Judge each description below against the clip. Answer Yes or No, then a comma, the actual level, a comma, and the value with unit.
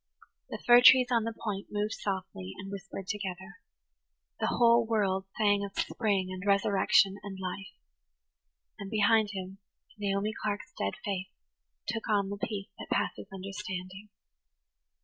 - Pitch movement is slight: Yes, narrow, 1.7 semitones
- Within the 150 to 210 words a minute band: No, average, 140 wpm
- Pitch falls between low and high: No, high, 200 Hz